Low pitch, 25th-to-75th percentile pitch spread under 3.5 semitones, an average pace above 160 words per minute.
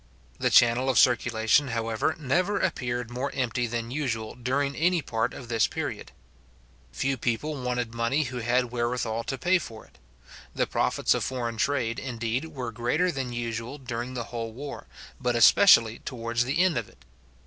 Yes: low, 125 Hz; average, 2.8 semitones; average, 170 wpm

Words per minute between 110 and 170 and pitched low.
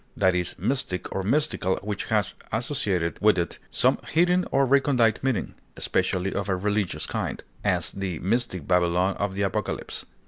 Yes: average, 160 wpm; low, 100 Hz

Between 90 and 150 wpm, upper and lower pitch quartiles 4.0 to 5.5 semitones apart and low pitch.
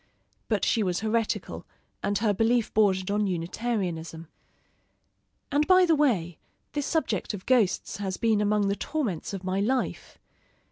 No: average, 145 wpm; average, 4.3 semitones; high, 210 Hz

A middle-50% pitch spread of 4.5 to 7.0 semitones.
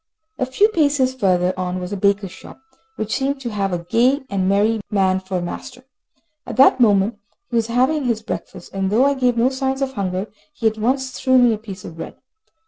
Yes: average, 5.2 semitones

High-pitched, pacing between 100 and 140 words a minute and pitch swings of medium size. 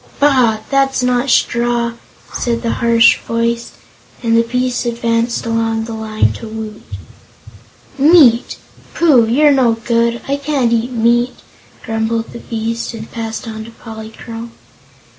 No: high, 235 Hz; slow, 135 wpm; narrow, 1.4 semitones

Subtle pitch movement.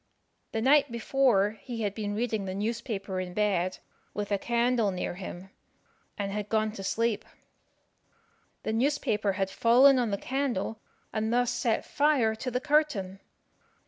No: average, 3.6 semitones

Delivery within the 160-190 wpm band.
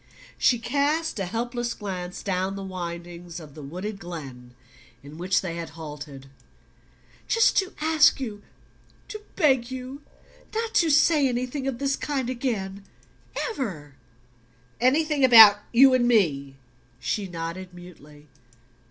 No: slow, 135 wpm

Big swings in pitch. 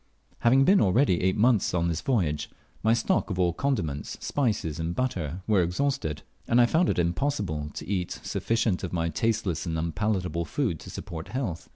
Yes: wide, 5.9 semitones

